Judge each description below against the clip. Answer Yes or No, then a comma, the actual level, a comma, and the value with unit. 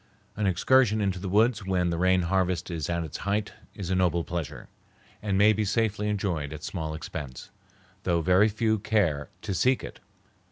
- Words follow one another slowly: No, average, 185 wpm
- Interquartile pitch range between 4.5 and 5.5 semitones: No, average, 3.6 semitones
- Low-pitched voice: Yes, very low, 95 Hz